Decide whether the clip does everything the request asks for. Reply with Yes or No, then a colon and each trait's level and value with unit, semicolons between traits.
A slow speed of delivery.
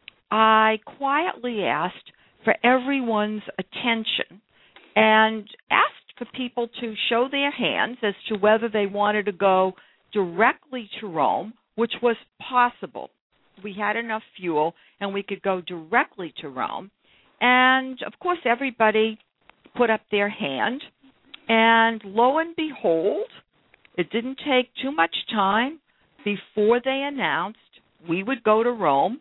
Yes: slow, 130 wpm